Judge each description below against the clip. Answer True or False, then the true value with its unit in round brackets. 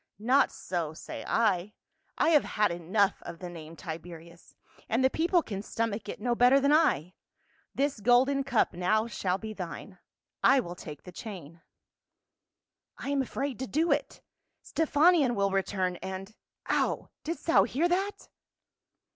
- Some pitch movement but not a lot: False (7.3 semitones)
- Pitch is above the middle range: True (215 Hz)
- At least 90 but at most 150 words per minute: False (160 wpm)